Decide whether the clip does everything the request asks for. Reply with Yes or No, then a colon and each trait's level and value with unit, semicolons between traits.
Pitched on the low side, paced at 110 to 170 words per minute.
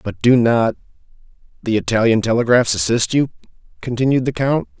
Yes: low, 115 Hz; average, 140 wpm